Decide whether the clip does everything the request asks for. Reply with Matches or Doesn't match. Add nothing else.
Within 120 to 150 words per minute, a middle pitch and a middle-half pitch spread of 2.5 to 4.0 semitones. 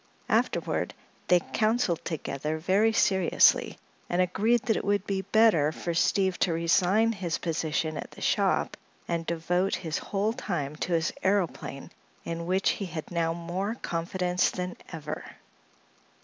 Matches